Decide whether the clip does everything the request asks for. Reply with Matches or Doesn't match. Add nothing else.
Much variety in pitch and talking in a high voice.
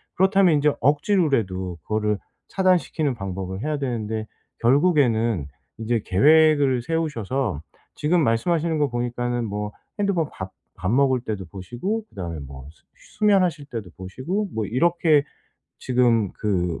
Doesn't match